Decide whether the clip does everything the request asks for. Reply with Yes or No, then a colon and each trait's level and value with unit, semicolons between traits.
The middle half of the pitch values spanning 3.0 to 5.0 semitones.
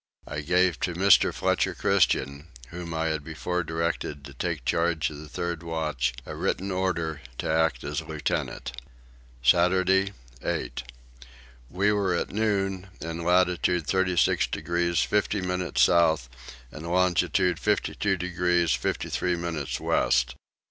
No: narrow, 2.4 semitones